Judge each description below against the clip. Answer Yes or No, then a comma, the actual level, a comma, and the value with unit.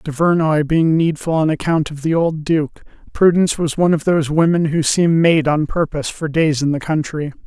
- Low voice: No, medium, 155 Hz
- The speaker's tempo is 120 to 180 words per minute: No, average, 200 wpm